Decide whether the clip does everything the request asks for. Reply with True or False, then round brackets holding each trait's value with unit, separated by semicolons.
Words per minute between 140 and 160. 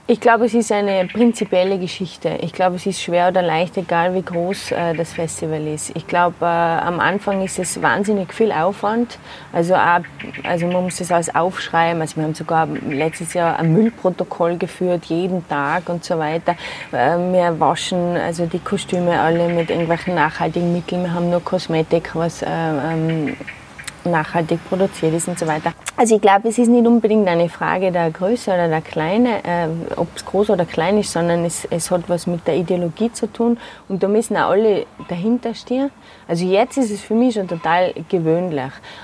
False (190 wpm)